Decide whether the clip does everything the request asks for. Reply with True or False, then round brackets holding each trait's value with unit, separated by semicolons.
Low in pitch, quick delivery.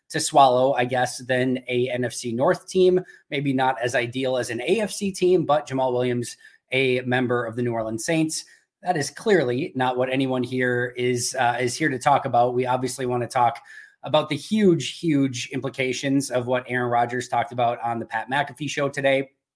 False (130 Hz; 195 wpm)